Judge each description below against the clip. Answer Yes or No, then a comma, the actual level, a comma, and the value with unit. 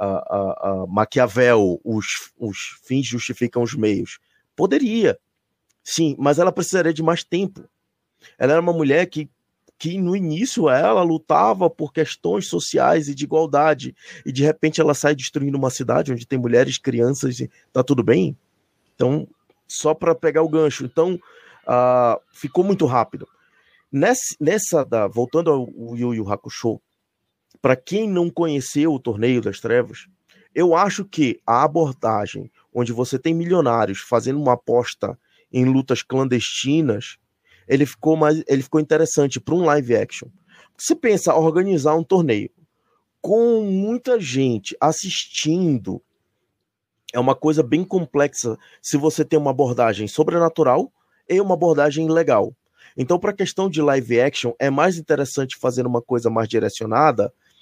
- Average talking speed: Yes, average, 150 wpm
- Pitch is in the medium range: Yes, medium, 150 Hz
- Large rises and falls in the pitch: No, average, 4.9 semitones